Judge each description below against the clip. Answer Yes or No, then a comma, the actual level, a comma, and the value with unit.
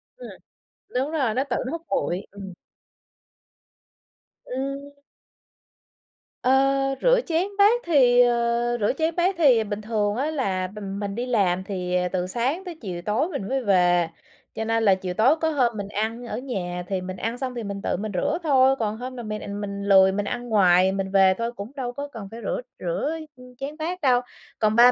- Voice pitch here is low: No, high, 230 Hz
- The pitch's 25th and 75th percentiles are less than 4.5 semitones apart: No, average, 5.3 semitones